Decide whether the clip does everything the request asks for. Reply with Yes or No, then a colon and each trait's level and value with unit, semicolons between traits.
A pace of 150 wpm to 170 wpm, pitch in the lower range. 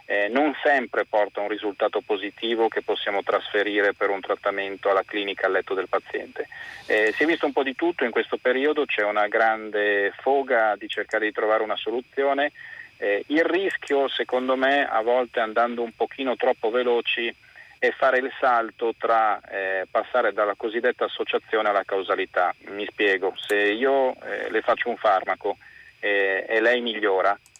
Yes: average, 165 wpm; low, 125 Hz